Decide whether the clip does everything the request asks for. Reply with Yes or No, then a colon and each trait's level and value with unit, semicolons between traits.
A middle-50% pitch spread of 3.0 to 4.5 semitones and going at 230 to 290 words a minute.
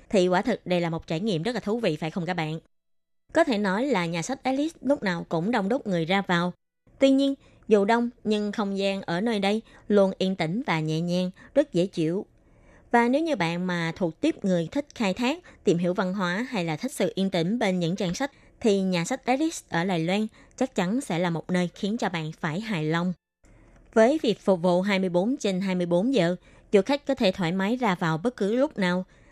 No: average, 5.1 semitones; average, 235 wpm